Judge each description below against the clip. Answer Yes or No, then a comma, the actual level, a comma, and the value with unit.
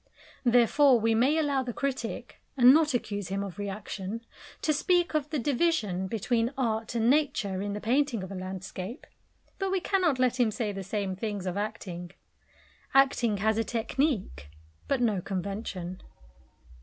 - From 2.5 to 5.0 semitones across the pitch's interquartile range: No, wide, 5.4 semitones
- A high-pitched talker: Yes, high, 225 Hz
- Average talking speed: Yes, average, 160 wpm